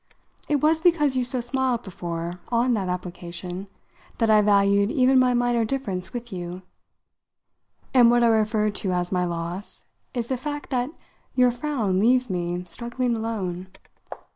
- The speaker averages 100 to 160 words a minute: Yes, average, 155 wpm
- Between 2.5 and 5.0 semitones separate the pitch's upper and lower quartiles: No, wide, 5.4 semitones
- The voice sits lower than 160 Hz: No, high, 225 Hz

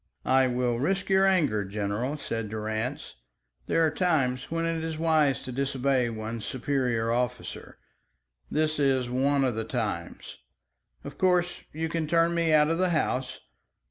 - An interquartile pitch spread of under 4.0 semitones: No, average, 5.1 semitones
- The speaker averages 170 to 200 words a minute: No, average, 155 wpm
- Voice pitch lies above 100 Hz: Yes, low, 135 Hz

